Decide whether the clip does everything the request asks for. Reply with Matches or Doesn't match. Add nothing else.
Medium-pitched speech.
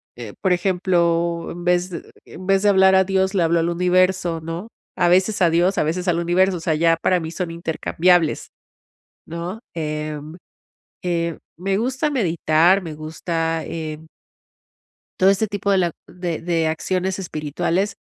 Matches